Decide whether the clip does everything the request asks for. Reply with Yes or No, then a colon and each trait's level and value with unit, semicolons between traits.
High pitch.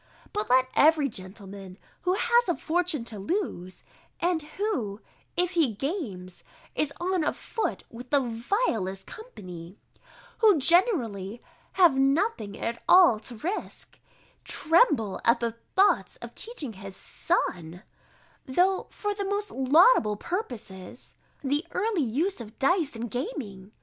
Yes: very high, 270 Hz